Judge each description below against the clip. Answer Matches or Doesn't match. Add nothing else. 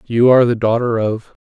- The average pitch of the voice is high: Doesn't match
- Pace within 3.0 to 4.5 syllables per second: Doesn't match